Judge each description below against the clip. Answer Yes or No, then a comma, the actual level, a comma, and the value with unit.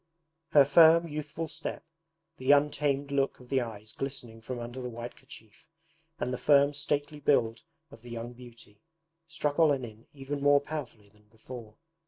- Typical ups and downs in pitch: Yes, average, 3.7 semitones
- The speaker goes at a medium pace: Yes, average, 160 wpm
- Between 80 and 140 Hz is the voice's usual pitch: Yes, low, 135 Hz